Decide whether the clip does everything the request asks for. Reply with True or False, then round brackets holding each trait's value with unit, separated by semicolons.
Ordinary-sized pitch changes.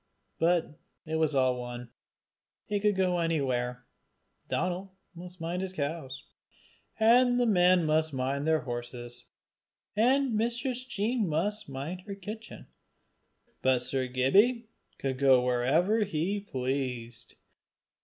False (7.8 semitones)